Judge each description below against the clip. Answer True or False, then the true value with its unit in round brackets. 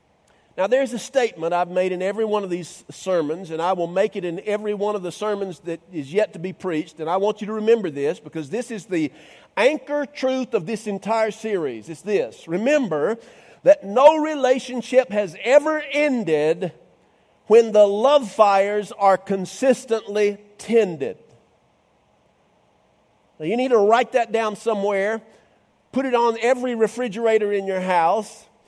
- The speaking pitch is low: False (210 Hz)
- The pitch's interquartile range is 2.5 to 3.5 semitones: False (4.1 semitones)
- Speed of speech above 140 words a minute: True (165 wpm)